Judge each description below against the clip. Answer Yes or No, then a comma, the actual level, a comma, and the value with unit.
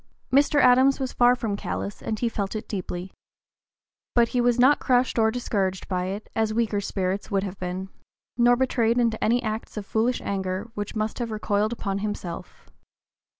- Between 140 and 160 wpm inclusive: No, average, 180 wpm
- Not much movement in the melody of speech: No, average, 3.5 semitones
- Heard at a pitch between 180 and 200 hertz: No, high, 220 Hz